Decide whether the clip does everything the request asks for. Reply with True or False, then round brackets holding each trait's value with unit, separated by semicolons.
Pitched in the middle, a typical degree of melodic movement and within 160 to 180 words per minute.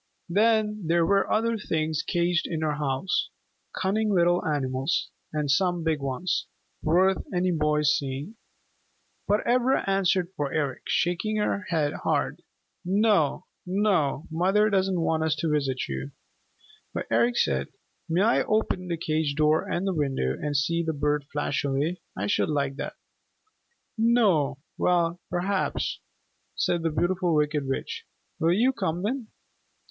False (170 Hz; 4.6 semitones; 145 wpm)